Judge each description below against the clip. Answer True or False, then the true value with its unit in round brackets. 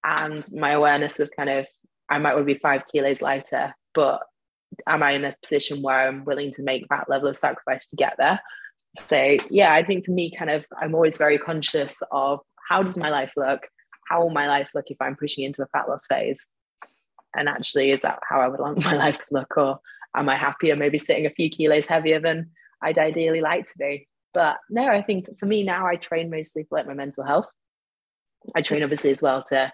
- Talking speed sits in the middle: False (230 wpm)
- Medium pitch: True (150 Hz)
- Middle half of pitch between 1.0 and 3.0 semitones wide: True (2.6 semitones)